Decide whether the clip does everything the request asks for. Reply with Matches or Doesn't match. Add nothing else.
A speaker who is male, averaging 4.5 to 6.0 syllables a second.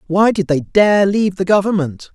Matches